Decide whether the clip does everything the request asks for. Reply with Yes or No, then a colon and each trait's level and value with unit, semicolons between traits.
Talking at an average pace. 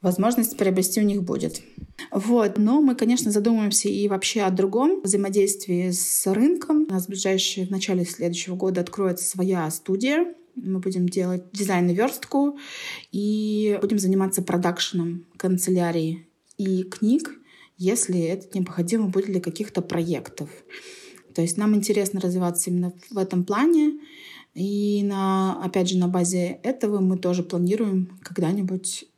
Yes: average, 140 wpm